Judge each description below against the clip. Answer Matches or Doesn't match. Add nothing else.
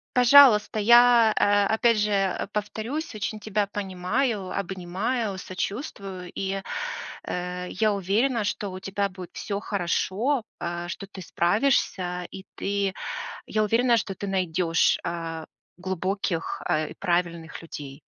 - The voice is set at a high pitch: Matches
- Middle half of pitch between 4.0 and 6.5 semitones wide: Doesn't match